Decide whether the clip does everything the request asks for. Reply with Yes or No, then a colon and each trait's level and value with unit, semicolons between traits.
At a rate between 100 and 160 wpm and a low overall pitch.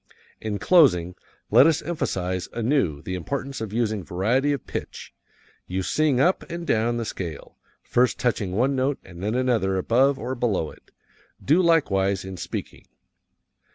Yes: average, 155 wpm; low, 115 Hz